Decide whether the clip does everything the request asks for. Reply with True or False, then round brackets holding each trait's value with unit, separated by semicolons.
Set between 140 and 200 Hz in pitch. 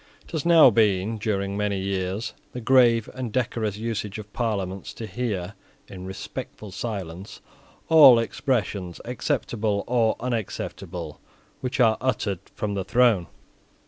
False (110 Hz)